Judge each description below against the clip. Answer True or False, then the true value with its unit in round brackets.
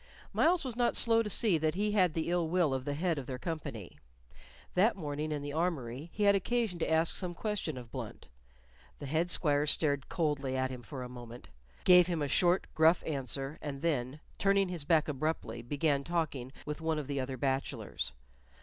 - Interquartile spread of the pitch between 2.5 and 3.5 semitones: False (4.5 semitones)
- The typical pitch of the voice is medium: True (155 Hz)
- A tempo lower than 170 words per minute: False (200 wpm)